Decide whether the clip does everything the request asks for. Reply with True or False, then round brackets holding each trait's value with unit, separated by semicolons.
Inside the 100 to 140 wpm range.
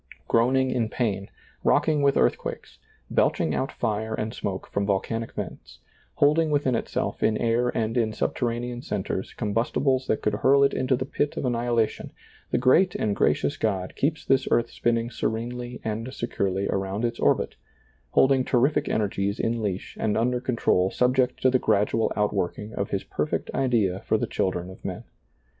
False (165 wpm)